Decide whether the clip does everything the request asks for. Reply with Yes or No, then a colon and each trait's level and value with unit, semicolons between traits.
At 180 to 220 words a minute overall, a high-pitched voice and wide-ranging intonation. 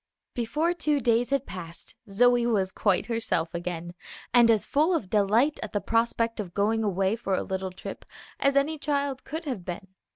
Yes: average, 185 wpm; high, 230 Hz; wide, 6.3 semitones